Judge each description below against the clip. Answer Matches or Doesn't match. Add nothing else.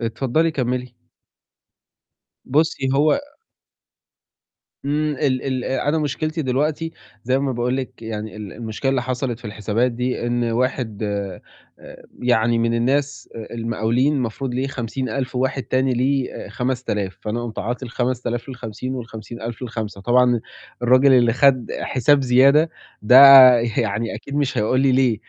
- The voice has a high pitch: Doesn't match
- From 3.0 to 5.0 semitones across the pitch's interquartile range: Doesn't match